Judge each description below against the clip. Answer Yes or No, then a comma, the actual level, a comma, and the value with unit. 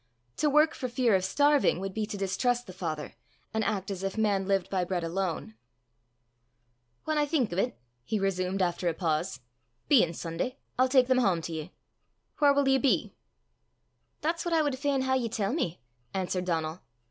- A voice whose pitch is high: Yes, high, 200 Hz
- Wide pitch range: Yes, wide, 6.4 semitones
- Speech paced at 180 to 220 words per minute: Yes, average, 190 wpm